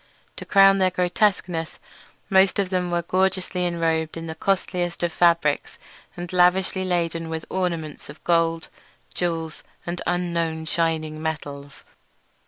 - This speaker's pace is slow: Yes, slow, 130 wpm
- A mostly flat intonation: Yes, narrow, 2.0 semitones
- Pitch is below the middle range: No, medium, 170 Hz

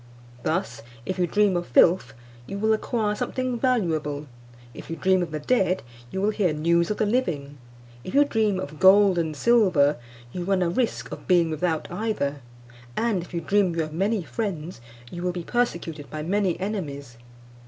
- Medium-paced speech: Yes, average, 185 wpm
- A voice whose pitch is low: No, medium, 180 Hz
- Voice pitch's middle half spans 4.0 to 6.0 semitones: Yes, average, 4.6 semitones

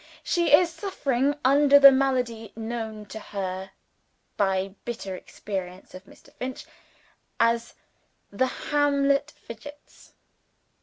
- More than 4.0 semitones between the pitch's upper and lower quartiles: Yes, wide, 5.6 semitones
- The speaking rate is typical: No, slow, 105 wpm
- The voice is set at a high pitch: Yes, high, 240 Hz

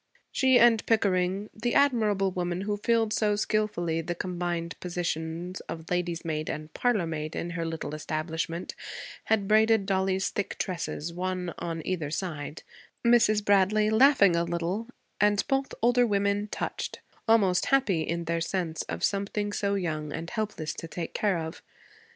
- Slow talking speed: No, average, 150 wpm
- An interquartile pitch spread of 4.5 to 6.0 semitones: No, average, 4.1 semitones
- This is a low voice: No, medium, 185 Hz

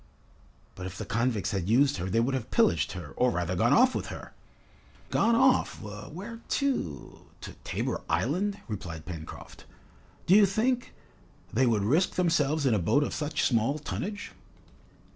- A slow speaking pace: No, average, 160 wpm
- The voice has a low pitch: Yes, low, 130 Hz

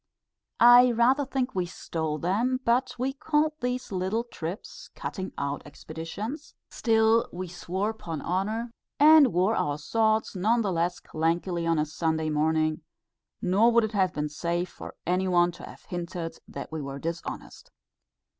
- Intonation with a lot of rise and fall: Yes, wide, 6.0 semitones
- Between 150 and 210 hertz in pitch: Yes, medium, 185 Hz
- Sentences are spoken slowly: No, average, 155 wpm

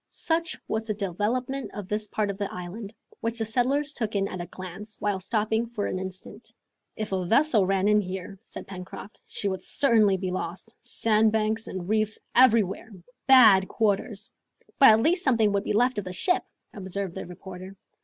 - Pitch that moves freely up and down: No, average, 3.0 semitones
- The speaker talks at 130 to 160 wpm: No, average, 185 wpm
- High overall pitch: Yes, high, 210 Hz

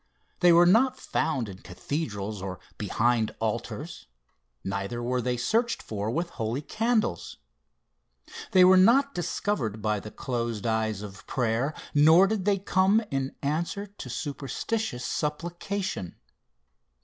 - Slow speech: Yes, slow, 125 wpm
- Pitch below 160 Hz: Yes, medium, 140 Hz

